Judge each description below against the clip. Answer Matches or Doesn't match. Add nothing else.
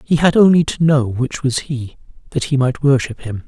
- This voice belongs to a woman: Doesn't match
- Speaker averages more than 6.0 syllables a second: Doesn't match